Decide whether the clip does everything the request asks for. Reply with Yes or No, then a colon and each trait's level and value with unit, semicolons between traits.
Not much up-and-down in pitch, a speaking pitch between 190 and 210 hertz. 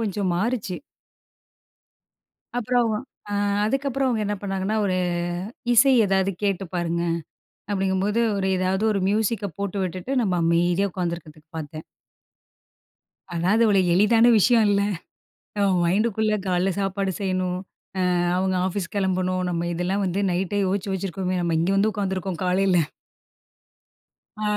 Yes: narrow, 2.2 semitones; high, 195 Hz